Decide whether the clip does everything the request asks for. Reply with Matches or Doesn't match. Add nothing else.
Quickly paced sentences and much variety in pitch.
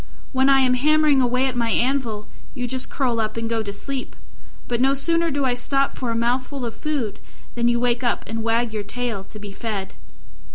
Doesn't match